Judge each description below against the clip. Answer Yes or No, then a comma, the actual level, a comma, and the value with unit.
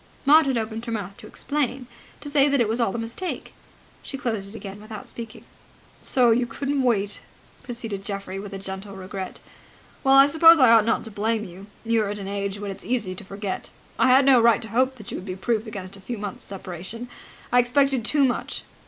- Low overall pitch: No, high, 225 Hz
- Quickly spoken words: Yes, fast, 220 wpm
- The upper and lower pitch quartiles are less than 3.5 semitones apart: No, average, 4.2 semitones